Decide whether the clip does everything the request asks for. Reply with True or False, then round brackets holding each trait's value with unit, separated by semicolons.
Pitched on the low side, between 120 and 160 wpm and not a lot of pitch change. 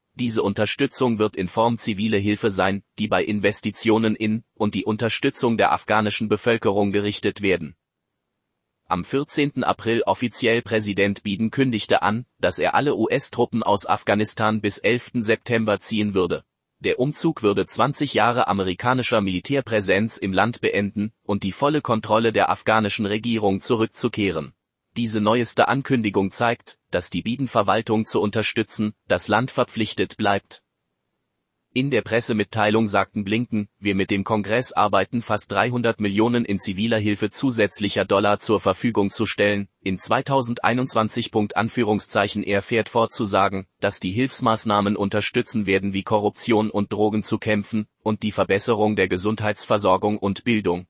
True (110 Hz; 135 wpm; 2.3 semitones)